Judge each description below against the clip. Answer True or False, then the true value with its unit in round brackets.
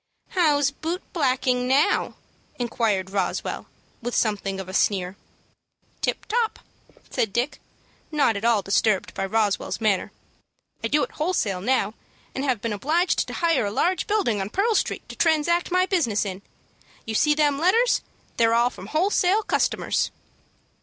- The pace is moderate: True (155 wpm)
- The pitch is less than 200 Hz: False (255 Hz)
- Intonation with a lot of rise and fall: True (8.2 semitones)